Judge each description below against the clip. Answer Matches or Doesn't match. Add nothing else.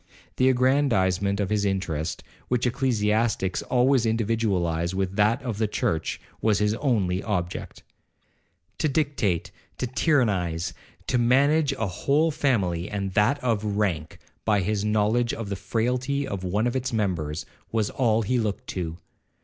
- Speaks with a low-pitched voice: Matches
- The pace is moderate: Matches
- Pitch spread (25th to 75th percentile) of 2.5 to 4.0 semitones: Doesn't match